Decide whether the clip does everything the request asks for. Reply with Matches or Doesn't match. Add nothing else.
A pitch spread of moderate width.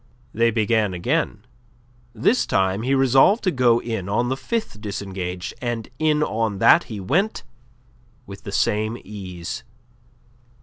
Matches